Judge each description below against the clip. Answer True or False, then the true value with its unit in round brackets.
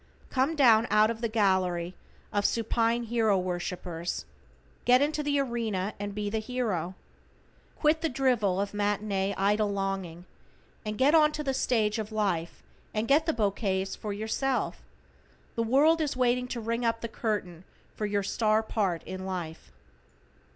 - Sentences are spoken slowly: False (155 wpm)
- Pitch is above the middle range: True (215 Hz)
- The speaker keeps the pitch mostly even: False (4.0 semitones)